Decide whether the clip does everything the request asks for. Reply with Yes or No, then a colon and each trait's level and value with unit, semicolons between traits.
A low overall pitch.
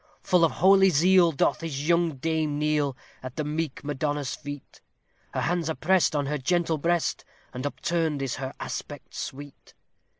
No: medium, 155 Hz